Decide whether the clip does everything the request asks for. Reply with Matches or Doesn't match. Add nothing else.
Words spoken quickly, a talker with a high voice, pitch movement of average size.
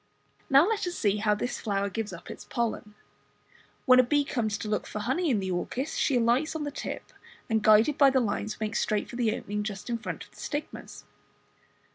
Matches